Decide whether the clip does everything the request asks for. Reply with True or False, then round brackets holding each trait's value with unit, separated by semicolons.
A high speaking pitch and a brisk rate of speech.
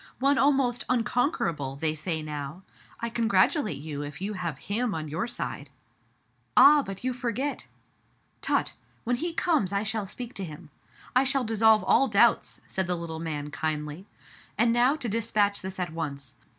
False (200 Hz; 175 wpm)